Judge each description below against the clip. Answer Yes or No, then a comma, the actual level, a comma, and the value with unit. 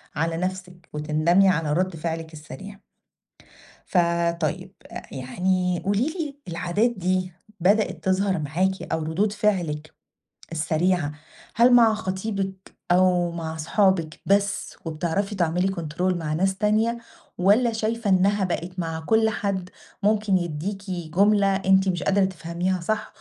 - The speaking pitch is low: No, medium, 185 Hz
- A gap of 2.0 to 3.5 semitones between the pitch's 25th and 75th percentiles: Yes, average, 3.0 semitones